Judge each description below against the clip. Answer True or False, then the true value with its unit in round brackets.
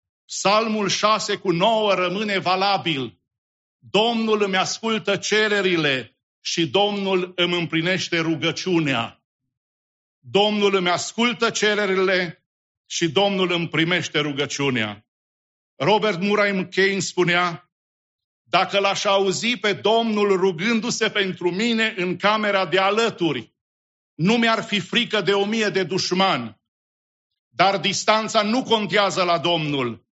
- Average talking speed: False (110 wpm)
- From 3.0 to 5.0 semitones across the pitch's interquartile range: True (4.0 semitones)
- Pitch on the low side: False (190 Hz)